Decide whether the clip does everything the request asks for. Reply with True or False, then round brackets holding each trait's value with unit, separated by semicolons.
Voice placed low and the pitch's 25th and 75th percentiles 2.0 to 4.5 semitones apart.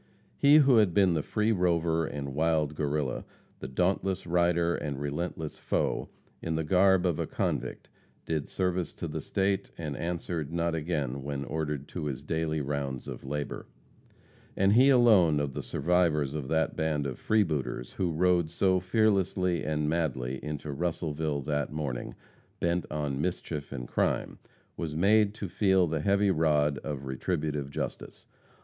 True (80 Hz; 3.8 semitones)